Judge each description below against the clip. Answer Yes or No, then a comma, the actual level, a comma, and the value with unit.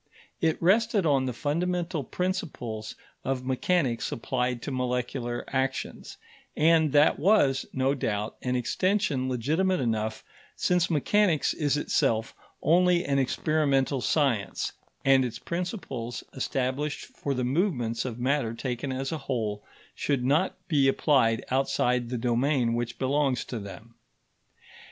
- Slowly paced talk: Yes, slow, 130 wpm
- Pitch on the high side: No, low, 135 Hz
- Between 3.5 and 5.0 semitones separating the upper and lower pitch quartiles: Yes, average, 4.2 semitones